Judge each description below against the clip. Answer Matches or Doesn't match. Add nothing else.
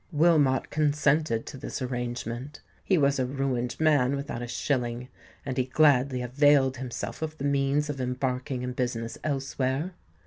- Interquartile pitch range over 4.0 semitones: Doesn't match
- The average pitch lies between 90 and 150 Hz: Matches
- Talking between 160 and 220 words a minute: Doesn't match